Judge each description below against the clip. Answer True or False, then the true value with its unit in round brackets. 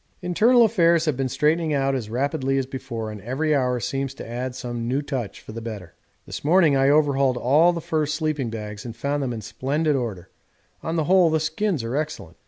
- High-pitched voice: False (135 Hz)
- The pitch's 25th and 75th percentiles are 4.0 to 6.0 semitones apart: True (4.5 semitones)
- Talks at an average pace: False (210 wpm)